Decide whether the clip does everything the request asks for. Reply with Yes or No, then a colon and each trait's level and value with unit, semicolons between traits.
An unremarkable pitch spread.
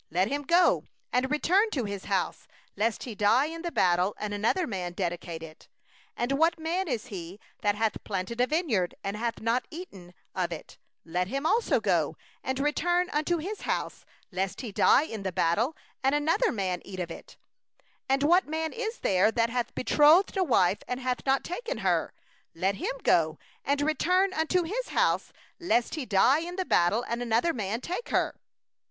No: wide, 8.7 semitones